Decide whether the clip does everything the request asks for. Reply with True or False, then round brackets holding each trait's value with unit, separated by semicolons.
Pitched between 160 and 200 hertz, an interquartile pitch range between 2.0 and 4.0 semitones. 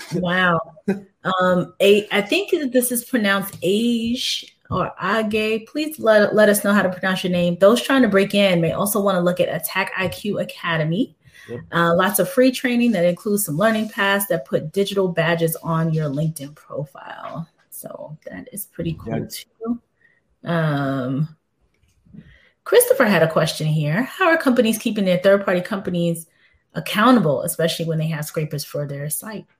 False (190 Hz; 4.7 semitones)